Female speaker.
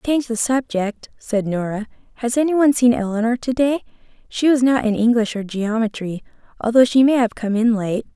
Yes: female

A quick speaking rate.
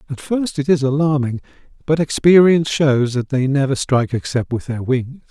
No: average, 180 wpm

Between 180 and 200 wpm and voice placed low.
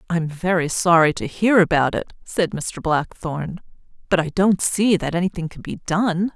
No: average, 190 wpm; medium, 175 Hz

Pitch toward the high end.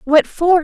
Yes: very high, 330 Hz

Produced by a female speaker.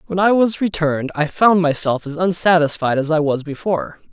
No: male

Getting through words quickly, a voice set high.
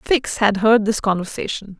No: average, 165 wpm; high, 210 Hz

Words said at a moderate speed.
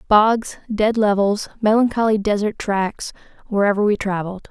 No: slow, 120 wpm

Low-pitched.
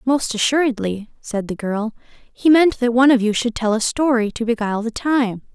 No: high, 235 Hz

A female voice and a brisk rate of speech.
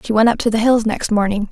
Yes: female; fast, 315 wpm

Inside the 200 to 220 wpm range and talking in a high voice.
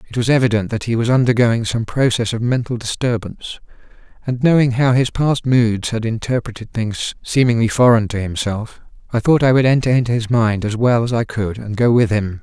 No: fast, 205 wpm; low, 115 Hz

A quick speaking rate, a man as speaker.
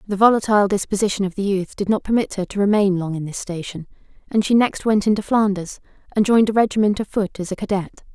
No: fast, 230 wpm; female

